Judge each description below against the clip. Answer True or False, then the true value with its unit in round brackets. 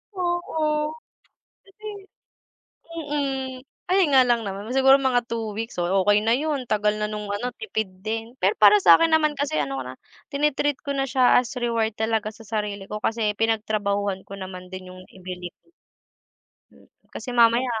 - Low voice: False (225 Hz)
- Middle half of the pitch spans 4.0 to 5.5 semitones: True (4.9 semitones)